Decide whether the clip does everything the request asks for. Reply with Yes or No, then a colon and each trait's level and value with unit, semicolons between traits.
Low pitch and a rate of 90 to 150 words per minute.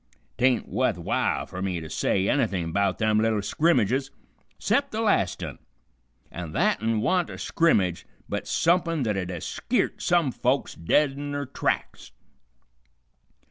Yes: low, 115 Hz; average, 145 wpm